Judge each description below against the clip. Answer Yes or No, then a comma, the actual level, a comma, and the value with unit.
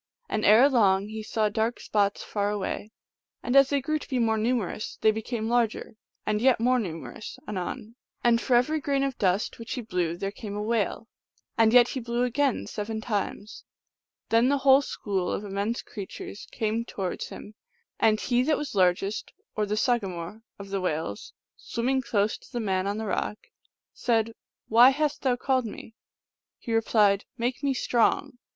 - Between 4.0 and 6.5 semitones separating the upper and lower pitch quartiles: No, average, 3.2 semitones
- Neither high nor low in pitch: No, high, 220 Hz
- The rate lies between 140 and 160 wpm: No, average, 185 wpm